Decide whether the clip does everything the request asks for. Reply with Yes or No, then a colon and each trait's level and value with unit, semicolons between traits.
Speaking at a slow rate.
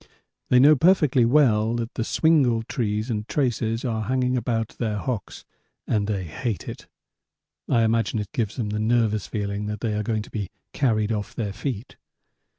No: average, 170 wpm